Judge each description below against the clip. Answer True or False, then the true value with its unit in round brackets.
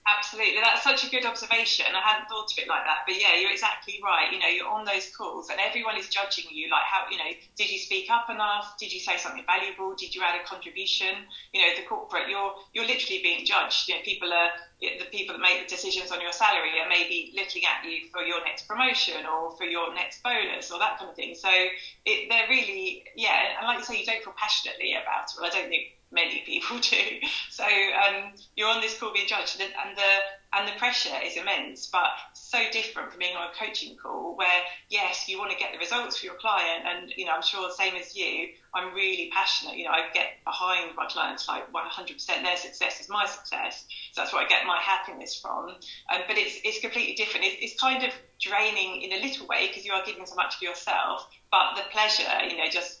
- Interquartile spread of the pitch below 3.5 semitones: False (4.4 semitones)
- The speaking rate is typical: False (240 wpm)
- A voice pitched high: True (200 Hz)